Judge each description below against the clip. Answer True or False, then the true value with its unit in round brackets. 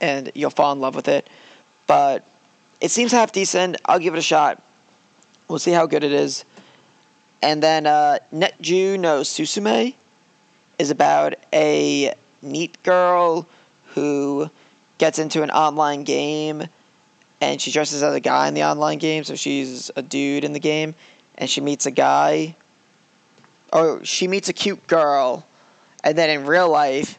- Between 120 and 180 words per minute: True (160 wpm)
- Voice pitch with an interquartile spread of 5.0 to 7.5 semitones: False (3.5 semitones)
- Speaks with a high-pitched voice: False (150 Hz)